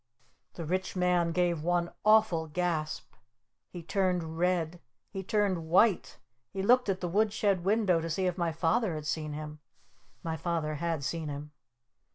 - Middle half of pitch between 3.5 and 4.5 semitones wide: No, average, 2.8 semitones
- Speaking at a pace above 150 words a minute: Yes, average, 165 wpm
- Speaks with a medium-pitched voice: Yes, medium, 175 Hz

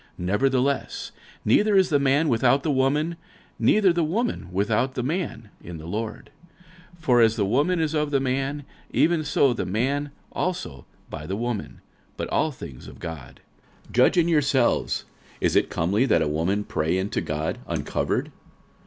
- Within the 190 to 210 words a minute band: No, average, 175 wpm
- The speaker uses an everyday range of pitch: No, wide, 6.8 semitones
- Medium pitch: No, low, 130 Hz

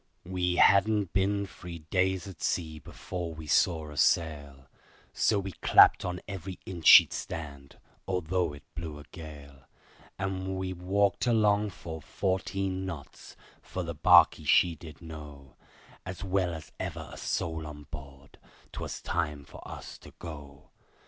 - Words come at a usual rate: Yes, average, 150 wpm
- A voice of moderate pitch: No, very low, 85 Hz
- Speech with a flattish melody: No, average, 3.8 semitones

